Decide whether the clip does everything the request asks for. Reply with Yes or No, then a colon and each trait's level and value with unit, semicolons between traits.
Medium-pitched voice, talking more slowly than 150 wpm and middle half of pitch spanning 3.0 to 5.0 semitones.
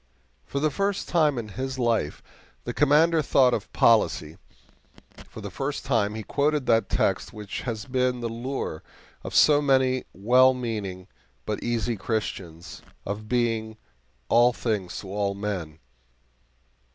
No: low, 115 Hz; average, 140 wpm; average, 4.1 semitones